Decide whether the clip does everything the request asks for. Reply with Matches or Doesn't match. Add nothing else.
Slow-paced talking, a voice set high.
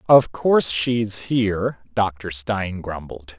Doesn't match